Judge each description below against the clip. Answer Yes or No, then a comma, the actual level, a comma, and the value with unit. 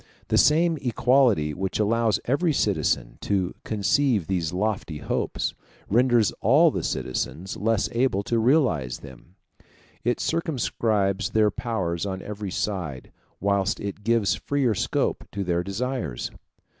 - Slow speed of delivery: Yes, slow, 130 wpm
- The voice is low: Yes, low, 105 Hz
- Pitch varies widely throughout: No, average, 4.6 semitones